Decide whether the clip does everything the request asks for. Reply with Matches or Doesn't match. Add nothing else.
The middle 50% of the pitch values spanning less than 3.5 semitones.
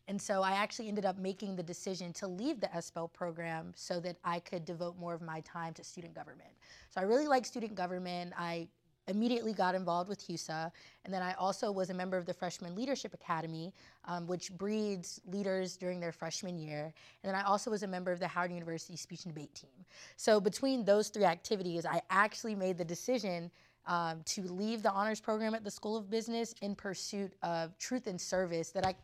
Matches